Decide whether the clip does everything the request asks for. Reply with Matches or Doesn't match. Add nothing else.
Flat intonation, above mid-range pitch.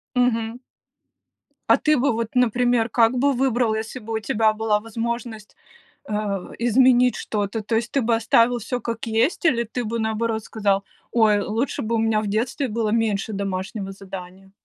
Matches